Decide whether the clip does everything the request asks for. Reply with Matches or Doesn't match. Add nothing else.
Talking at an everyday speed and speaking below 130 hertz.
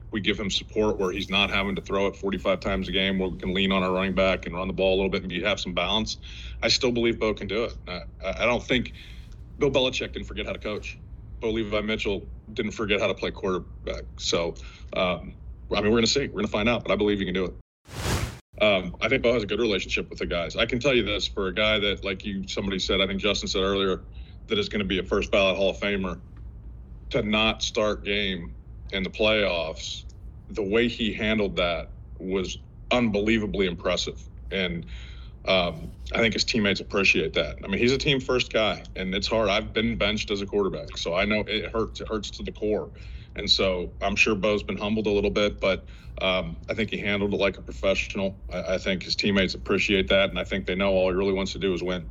Doesn't match